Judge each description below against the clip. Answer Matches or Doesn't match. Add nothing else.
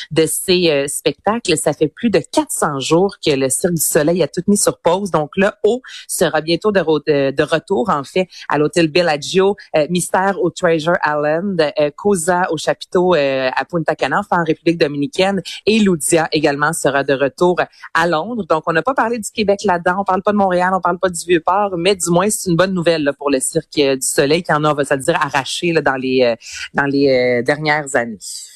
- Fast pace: Matches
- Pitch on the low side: Doesn't match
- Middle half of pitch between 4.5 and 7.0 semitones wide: Doesn't match